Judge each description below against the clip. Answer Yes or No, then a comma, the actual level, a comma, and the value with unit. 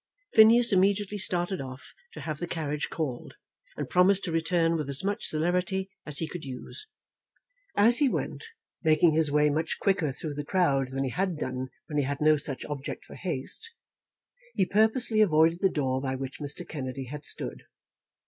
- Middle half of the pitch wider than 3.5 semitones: Yes, average, 5.1 semitones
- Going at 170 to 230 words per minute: Yes, average, 180 wpm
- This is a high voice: No, medium, 160 Hz